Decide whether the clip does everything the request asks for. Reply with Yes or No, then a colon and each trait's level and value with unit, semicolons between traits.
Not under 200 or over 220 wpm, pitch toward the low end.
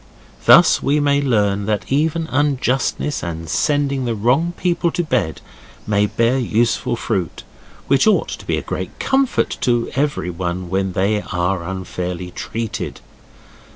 No: average, 140 wpm; low, 115 Hz